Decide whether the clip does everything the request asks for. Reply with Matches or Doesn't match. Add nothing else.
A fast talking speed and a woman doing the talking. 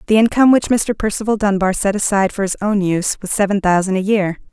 Matches